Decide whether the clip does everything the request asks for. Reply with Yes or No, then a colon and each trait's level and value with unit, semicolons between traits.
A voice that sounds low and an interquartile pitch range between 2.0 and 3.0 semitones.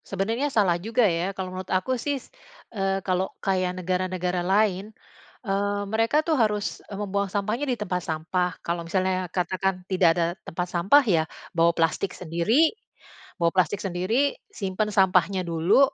No: high, 190 Hz; average, 2.7 semitones